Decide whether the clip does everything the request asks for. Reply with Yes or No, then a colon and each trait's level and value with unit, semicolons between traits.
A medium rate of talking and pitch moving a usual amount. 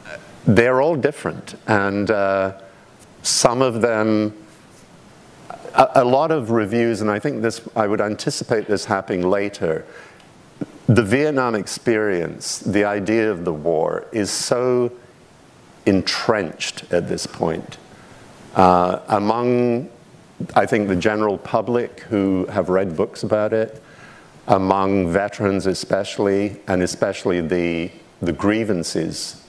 No: slow, 120 wpm; average, 3.4 semitones